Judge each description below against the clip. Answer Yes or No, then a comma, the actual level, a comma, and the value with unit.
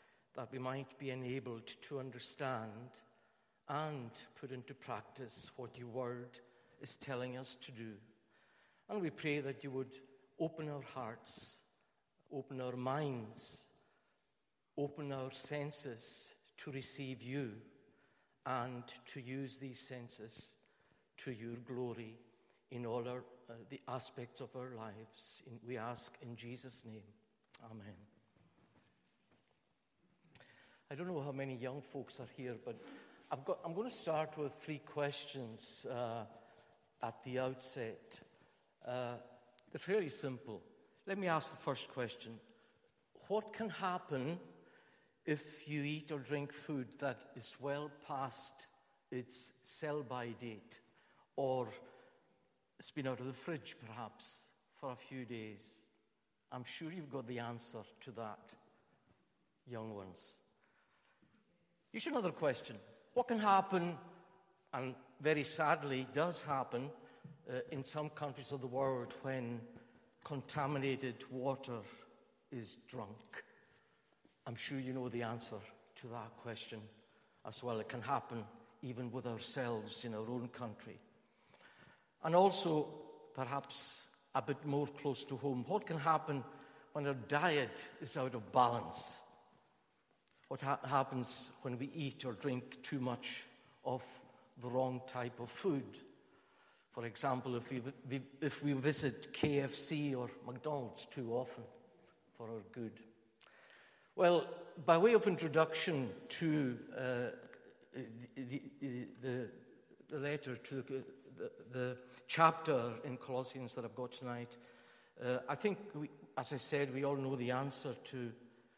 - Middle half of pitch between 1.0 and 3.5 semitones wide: Yes, average, 2.9 semitones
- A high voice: No, low, 130 Hz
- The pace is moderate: No, slow, 130 wpm